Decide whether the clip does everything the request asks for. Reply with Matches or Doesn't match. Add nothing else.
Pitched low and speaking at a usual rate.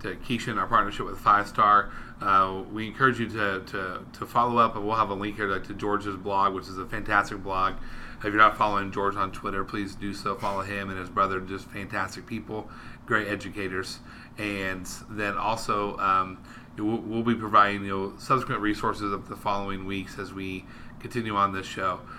Matches